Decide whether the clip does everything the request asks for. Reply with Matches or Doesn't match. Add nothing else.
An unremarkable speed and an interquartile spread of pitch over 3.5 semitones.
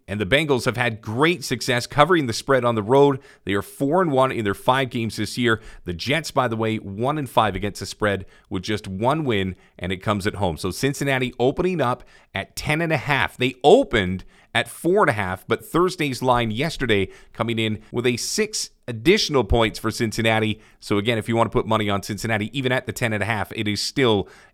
Doesn't match